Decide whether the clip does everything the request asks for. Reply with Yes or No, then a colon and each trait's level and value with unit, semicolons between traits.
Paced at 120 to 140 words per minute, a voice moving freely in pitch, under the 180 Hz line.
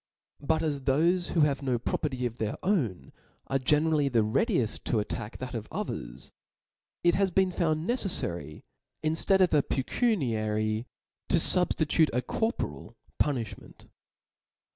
Yes: slow, 135 wpm; wide, 6.9 semitones; medium, 140 Hz